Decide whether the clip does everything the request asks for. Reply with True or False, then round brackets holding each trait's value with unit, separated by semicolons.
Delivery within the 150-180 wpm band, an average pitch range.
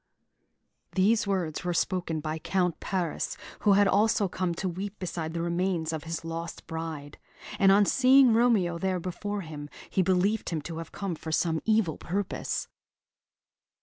True (160 wpm; 3.3 semitones)